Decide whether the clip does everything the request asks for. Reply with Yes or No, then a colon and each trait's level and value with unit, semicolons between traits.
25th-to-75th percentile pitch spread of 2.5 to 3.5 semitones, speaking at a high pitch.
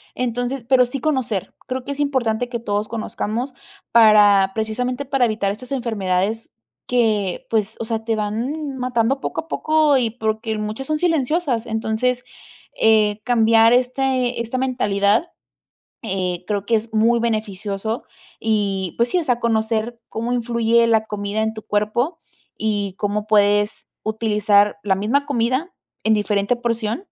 Yes: average, 2.8 semitones; high, 225 Hz